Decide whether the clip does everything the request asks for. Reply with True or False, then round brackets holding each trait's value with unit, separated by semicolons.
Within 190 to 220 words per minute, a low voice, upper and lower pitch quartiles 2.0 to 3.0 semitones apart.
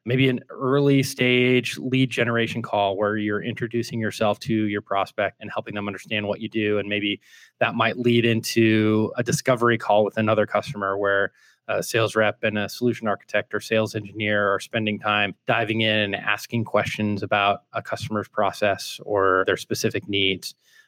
False (170 wpm; 110 Hz; 2.4 semitones)